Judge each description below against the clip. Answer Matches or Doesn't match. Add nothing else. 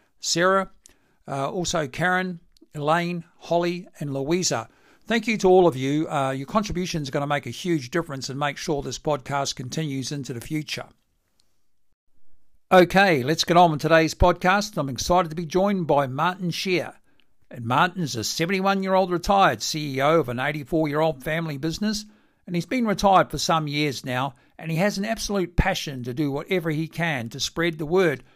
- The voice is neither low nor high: Matches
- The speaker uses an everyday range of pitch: Matches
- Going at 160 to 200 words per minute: Matches